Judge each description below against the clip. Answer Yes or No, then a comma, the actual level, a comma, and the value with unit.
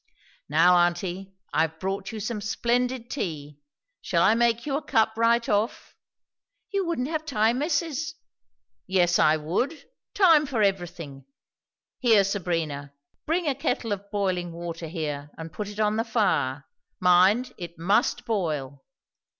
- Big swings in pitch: Yes, wide, 5.9 semitones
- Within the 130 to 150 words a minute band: Yes, average, 145 wpm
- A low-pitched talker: No, high, 200 Hz